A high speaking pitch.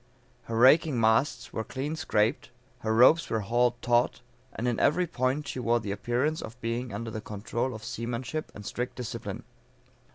No: low, 120 Hz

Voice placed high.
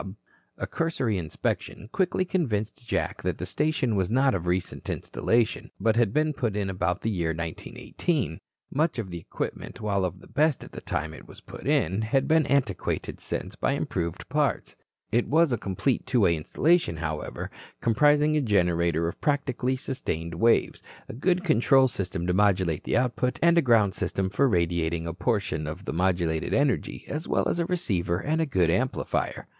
No: low, 110 Hz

